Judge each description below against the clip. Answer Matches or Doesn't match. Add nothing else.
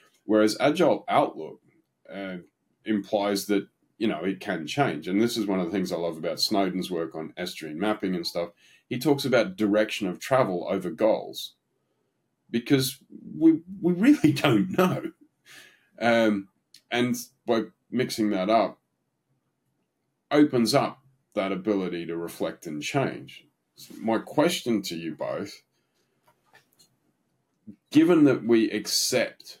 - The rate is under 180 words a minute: Matches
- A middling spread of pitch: Doesn't match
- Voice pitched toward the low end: Matches